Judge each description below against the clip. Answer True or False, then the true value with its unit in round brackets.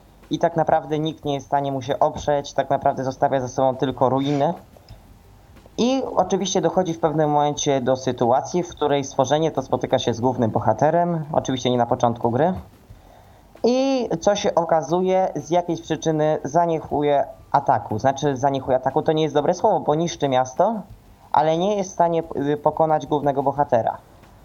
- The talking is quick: True (165 wpm)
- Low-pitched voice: False (145 Hz)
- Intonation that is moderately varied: True (3.7 semitones)